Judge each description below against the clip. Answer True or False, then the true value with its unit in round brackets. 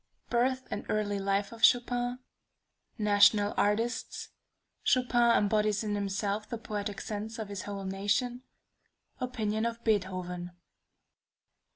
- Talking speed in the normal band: False (110 wpm)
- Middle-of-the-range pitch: False (210 Hz)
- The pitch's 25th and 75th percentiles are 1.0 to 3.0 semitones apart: True (2.5 semitones)